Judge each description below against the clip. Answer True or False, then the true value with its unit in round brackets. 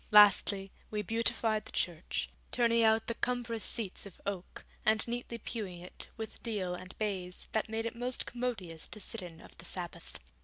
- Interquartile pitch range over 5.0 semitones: False (4.0 semitones)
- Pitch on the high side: True (215 Hz)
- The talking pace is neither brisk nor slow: True (180 wpm)